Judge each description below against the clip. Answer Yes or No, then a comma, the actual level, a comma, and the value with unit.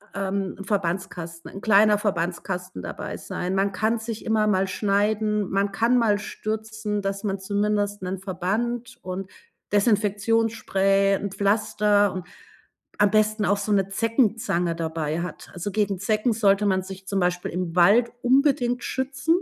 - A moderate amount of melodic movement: No, narrow, 2.3 semitones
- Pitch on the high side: Yes, high, 200 Hz